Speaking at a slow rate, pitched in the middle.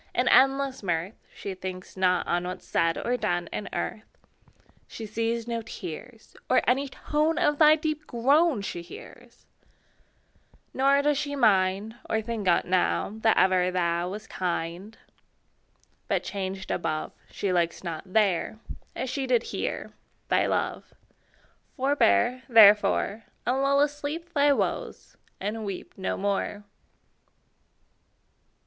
No: slow, 130 wpm; high, 215 Hz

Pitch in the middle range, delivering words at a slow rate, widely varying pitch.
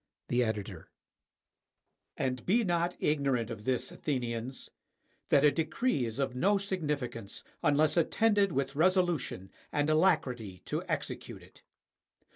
Yes: medium, 145 Hz; slow, 120 wpm; wide, 5.8 semitones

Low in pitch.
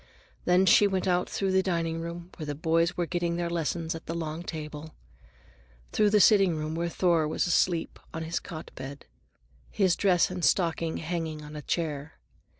No: medium, 170 Hz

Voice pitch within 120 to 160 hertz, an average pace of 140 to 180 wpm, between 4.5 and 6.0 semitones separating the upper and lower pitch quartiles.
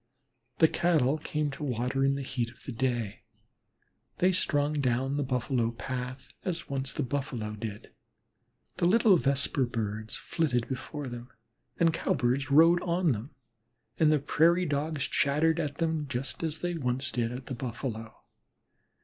No: low, 135 Hz; average, 155 wpm; average, 4.1 semitones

